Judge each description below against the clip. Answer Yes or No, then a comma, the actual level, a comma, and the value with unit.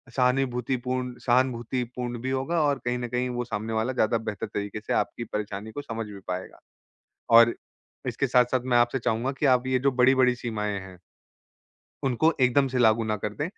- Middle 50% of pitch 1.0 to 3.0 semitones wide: Yes, narrow, 2.5 semitones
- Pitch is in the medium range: No, low, 125 Hz